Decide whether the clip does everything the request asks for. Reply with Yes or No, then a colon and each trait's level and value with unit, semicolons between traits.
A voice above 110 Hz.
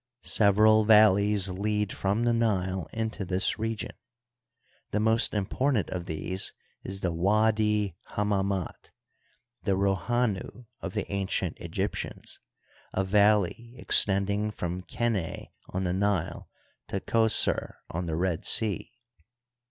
No: low, 100 Hz